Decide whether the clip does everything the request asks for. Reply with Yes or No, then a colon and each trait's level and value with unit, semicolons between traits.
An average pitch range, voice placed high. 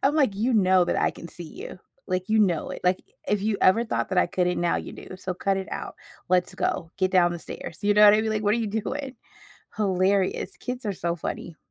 Yes: average, 3.0 semitones; high, 195 Hz